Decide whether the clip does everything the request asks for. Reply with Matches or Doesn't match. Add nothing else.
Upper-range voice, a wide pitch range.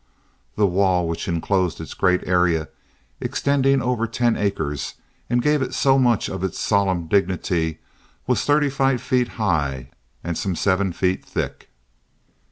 Doesn't match